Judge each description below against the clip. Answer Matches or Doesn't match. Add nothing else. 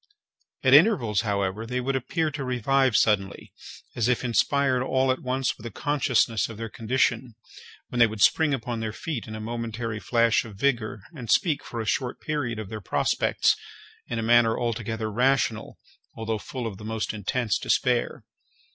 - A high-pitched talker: Doesn't match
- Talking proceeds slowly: Doesn't match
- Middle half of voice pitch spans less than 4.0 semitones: Matches